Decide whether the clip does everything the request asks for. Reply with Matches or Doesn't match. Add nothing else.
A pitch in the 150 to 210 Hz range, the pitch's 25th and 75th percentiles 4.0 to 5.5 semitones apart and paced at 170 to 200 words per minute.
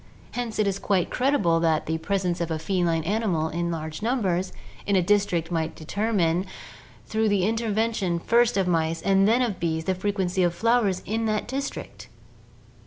Matches